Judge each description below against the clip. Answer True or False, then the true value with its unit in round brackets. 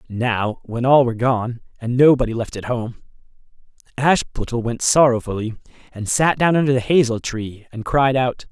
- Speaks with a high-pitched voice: False (125 Hz)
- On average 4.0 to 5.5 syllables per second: True (4.9 syllables/s)